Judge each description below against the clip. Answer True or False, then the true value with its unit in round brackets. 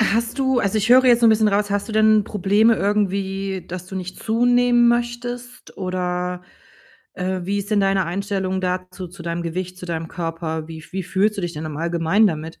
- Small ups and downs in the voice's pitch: False (3.4 semitones)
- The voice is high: True (195 Hz)